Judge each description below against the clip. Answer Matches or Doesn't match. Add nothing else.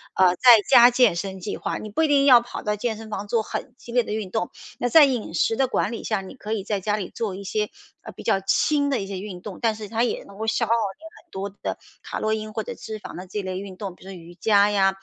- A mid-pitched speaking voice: Doesn't match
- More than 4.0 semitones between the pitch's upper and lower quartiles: Doesn't match